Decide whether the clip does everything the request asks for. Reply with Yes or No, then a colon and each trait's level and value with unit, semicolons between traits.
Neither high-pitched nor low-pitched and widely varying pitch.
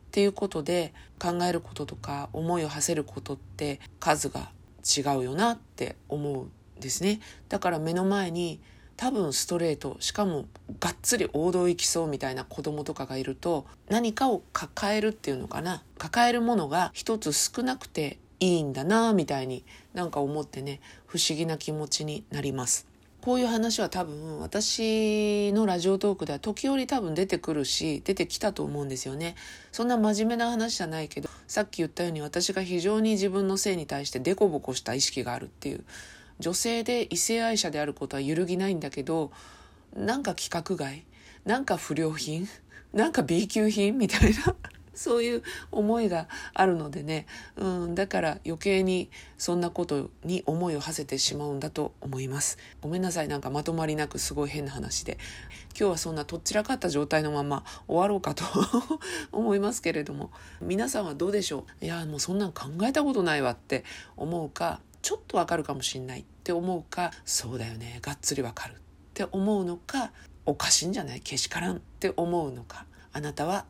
Yes: medium, 170 Hz; wide, 5.7 semitones